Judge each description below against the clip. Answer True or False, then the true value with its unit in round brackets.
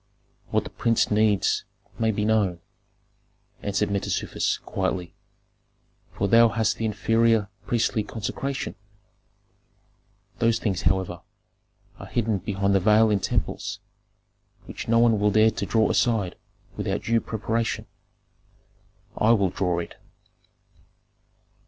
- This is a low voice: True (105 Hz)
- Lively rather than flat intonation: False (2.4 semitones)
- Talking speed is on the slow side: True (115 wpm)